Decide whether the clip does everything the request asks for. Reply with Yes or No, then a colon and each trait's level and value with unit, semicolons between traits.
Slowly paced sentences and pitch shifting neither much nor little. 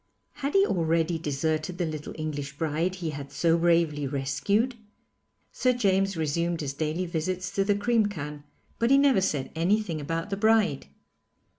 No: average, 160 wpm; average, 4.5 semitones